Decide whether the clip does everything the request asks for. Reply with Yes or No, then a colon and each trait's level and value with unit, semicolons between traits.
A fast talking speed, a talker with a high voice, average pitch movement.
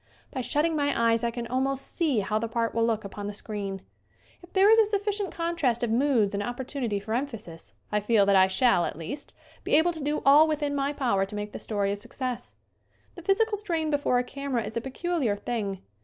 No: fast, 225 wpm; high, 245 Hz; wide, 6.0 semitones